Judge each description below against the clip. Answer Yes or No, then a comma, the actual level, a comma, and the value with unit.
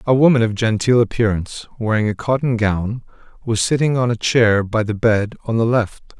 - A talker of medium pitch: No, low, 115 Hz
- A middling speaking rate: Yes, average, 195 wpm